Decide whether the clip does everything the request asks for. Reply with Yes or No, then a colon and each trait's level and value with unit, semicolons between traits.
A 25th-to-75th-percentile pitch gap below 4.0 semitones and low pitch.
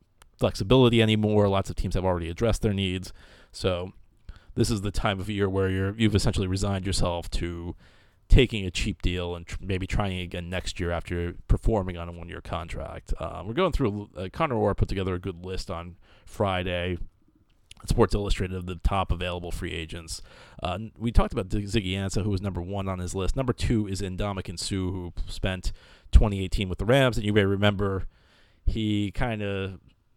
Yes: average, 2.8 semitones; very low, 95 Hz